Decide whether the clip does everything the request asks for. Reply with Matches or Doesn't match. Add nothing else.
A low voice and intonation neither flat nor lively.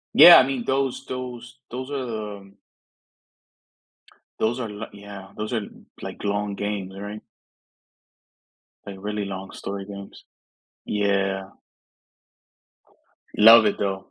Matches